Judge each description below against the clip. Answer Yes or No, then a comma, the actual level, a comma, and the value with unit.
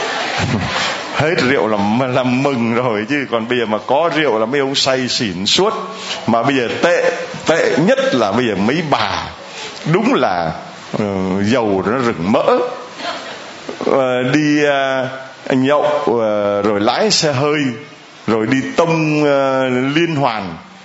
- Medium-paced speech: No, slow, 150 wpm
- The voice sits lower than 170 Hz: Yes, low, 135 Hz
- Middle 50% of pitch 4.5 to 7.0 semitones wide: No, average, 4.0 semitones